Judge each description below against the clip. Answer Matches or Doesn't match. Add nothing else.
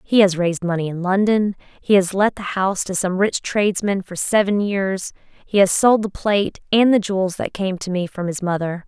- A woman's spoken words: Matches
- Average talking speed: Doesn't match